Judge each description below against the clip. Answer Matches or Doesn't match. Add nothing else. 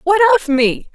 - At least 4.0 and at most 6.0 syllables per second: Doesn't match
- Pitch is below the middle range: Doesn't match